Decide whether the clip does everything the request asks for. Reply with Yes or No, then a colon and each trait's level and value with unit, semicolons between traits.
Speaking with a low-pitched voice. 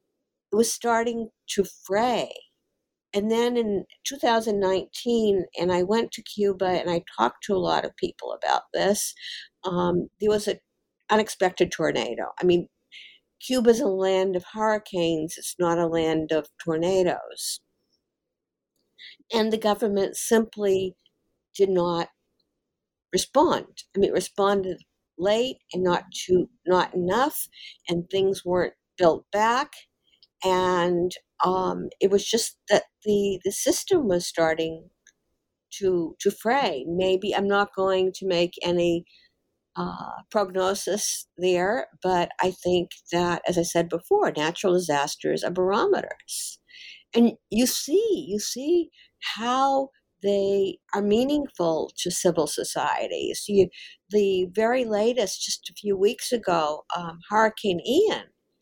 No: high, 195 Hz